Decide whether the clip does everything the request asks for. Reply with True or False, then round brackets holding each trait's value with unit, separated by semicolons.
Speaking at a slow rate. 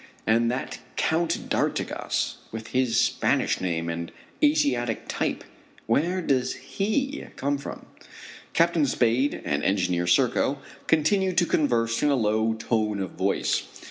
True (130 wpm)